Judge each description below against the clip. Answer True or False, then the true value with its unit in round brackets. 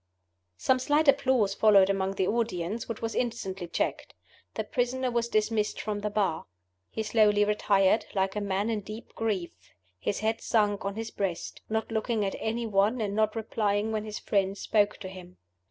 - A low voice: False (210 Hz)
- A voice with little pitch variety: True (2.3 semitones)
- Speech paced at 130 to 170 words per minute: False (180 wpm)